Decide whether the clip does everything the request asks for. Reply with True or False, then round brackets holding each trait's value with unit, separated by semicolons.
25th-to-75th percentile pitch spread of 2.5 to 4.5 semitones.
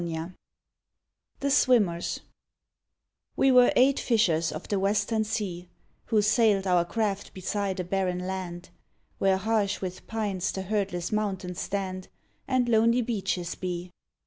True (3.3 semitones)